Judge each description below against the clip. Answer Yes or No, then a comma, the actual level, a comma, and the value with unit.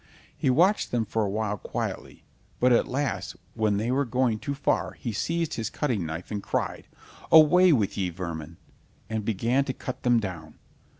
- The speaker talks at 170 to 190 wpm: Yes, average, 180 wpm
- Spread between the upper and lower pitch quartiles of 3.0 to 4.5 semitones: No, average, 4.9 semitones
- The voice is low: Yes, low, 115 Hz